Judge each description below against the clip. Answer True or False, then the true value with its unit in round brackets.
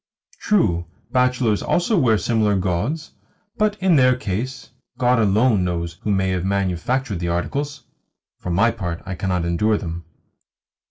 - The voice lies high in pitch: False (105 Hz)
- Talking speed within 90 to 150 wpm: True (145 wpm)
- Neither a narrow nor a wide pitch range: False (6.1 semitones)